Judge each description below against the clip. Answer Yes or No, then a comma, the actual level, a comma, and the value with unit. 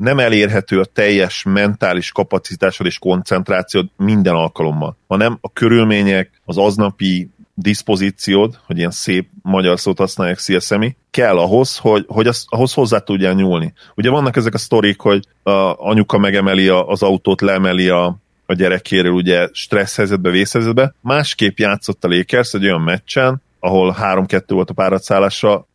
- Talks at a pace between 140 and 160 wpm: Yes, average, 145 wpm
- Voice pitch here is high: No, low, 100 Hz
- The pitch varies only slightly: No, average, 3.1 semitones